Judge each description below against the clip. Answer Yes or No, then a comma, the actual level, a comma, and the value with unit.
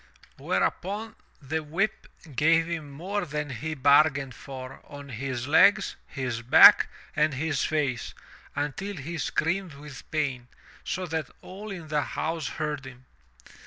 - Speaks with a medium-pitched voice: Yes, medium, 150 Hz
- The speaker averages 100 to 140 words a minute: Yes, slow, 135 wpm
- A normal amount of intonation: Yes, average, 3.3 semitones